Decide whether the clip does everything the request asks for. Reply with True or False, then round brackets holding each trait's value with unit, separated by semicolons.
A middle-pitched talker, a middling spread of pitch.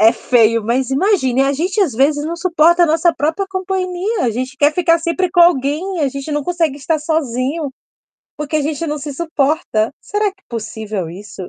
False (300 Hz; 4.6 semitones)